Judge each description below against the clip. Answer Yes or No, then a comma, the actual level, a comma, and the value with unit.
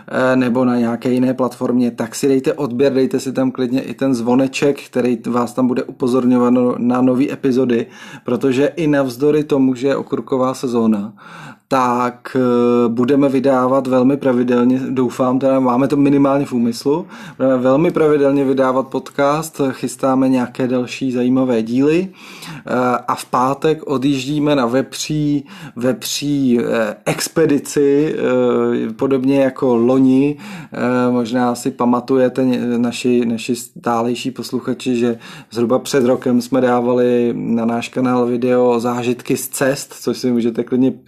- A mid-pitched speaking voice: No, low, 130 Hz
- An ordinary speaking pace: Yes, average, 130 wpm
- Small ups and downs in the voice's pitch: Yes, narrow, 1.9 semitones